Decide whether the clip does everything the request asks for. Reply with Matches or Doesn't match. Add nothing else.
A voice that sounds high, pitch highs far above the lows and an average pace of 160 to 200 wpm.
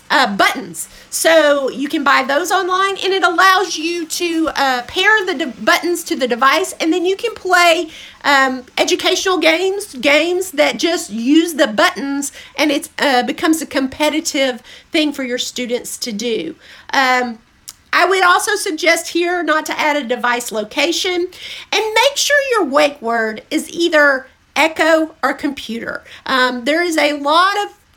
Doesn't match